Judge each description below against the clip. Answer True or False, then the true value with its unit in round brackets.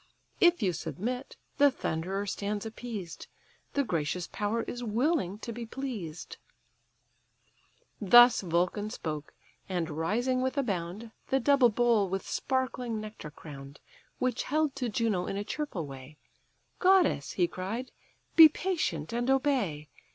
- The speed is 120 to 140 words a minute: True (135 wpm)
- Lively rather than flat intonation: True (6.4 semitones)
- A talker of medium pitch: False (215 Hz)